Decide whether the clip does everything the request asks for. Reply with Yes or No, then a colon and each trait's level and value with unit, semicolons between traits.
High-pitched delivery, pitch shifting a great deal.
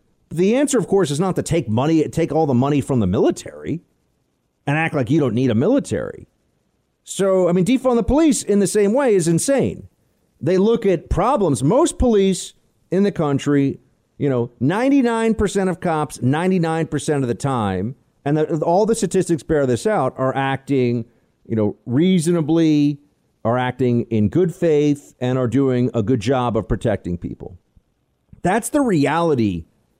No: medium, 155 Hz; wide, 6.8 semitones